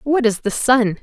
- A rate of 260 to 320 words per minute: No, fast, 235 wpm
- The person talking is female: Yes, female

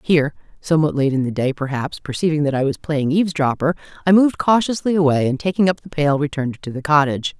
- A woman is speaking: Yes, female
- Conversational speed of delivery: No, fast, 210 wpm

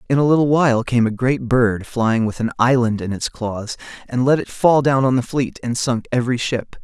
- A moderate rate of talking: No, fast, 235 wpm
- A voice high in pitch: No, low, 125 Hz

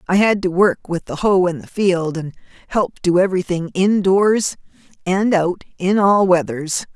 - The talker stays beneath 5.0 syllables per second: Yes, 4.5 syllables/s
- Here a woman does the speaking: Yes, female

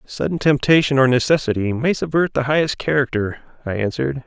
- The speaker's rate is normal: Yes, average, 155 wpm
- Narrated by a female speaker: No, male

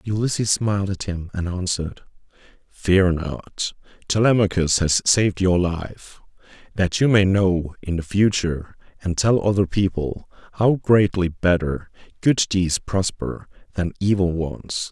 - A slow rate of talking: Yes, slow, 130 wpm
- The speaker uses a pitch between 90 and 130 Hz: Yes, very low, 95 Hz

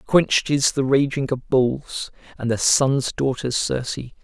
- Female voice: No, male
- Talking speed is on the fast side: No, average, 155 wpm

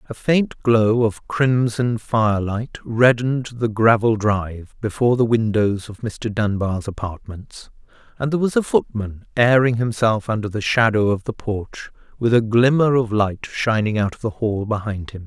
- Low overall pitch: Yes, low, 110 Hz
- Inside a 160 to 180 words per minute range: Yes, average, 165 wpm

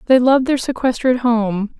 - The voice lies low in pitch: No, high, 245 Hz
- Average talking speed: Yes, average, 170 wpm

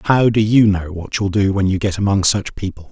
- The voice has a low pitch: Yes, low, 100 Hz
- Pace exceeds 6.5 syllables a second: No, 5.6 syllables/s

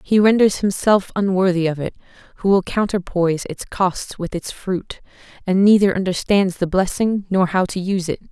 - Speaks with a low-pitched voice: No, high, 190 Hz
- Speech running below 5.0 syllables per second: No, 5.1 syllables/s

